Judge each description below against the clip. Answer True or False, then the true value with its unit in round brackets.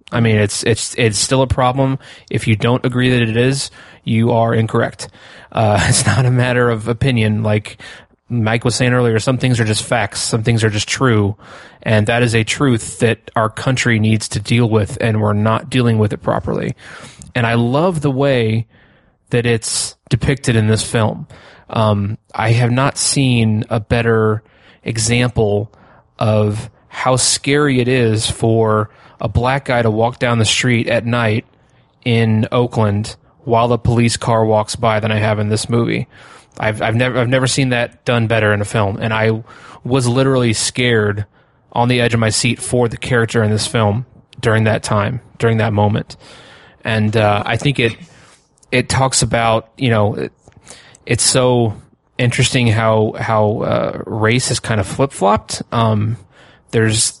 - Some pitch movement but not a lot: False (2.3 semitones)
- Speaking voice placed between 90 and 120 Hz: True (115 Hz)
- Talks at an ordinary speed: True (175 wpm)